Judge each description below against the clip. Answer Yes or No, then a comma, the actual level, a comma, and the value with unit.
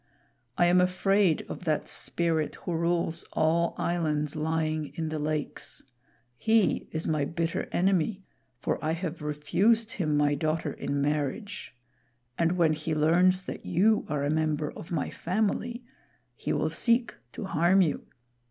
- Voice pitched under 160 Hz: No, medium, 165 Hz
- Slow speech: No, average, 150 wpm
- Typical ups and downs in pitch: Yes, average, 3.2 semitones